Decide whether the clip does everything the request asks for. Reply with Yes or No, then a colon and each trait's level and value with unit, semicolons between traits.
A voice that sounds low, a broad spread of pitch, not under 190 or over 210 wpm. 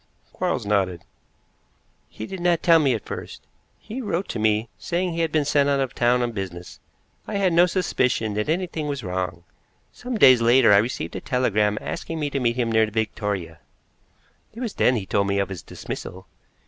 Yes: low, 120 Hz; wide, 7.9 semitones; average, 195 wpm